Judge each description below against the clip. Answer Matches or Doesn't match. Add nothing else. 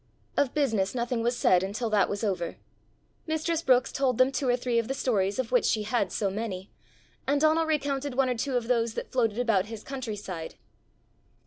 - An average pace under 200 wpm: Doesn't match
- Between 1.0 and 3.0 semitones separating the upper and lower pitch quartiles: Doesn't match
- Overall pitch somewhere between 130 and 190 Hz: Doesn't match